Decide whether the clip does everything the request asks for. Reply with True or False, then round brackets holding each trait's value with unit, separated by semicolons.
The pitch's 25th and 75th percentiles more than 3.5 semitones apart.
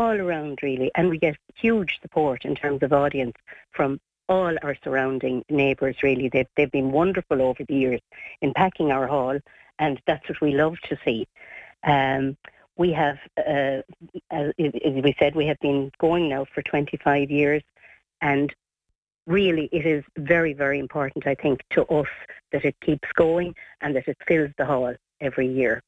False (2.8 semitones)